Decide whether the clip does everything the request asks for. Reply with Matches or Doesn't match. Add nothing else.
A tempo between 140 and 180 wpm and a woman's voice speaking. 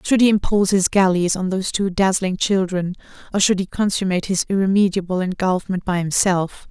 Matches